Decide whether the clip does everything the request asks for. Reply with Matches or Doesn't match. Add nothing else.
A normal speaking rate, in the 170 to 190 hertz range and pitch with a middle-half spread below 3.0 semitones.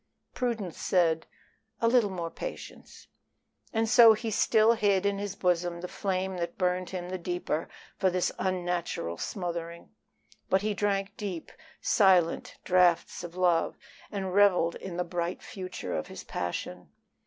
Matches